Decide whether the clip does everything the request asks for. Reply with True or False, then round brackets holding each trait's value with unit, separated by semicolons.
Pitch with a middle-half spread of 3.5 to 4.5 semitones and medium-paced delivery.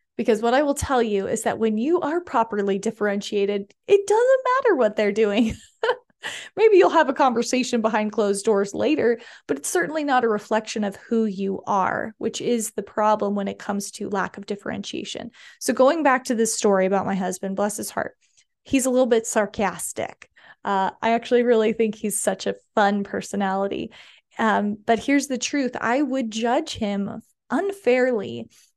True (4.0 semitones; 180 wpm)